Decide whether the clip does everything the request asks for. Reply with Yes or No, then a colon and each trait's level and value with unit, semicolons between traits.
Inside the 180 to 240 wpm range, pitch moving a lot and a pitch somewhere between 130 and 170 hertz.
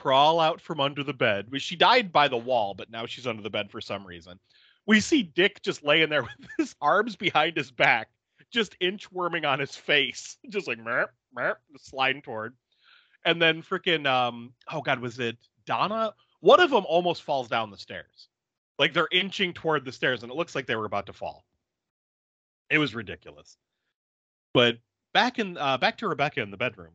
Yes: average, 195 wpm; wide, 6.9 semitones; medium, 140 Hz